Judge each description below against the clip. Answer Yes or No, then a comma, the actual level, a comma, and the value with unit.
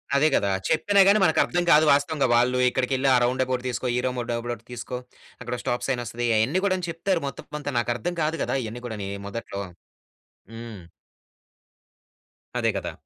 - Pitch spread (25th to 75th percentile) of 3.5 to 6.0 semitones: Yes, average, 4.2 semitones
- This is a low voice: Yes, low, 125 Hz